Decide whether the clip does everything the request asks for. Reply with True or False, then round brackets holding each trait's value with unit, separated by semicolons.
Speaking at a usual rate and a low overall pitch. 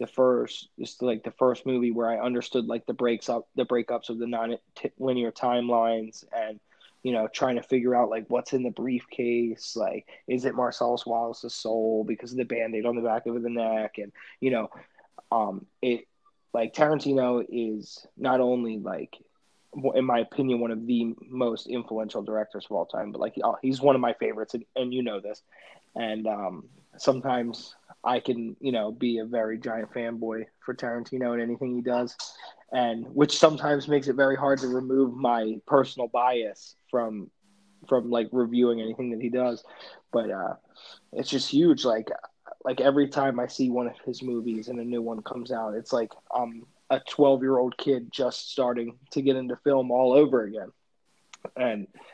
True (180 wpm; 120 Hz)